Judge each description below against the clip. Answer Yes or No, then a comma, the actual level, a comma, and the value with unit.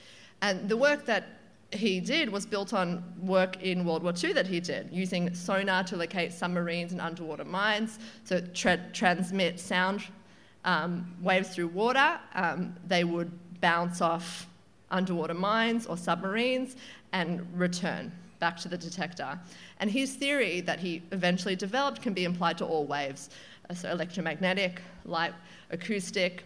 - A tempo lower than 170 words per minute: Yes, average, 145 wpm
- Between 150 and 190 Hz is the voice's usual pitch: Yes, medium, 185 Hz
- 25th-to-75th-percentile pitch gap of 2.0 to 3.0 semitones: Yes, narrow, 2.6 semitones